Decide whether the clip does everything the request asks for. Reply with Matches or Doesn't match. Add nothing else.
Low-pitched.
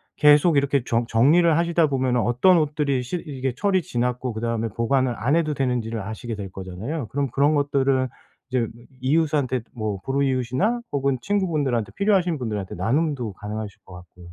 Matches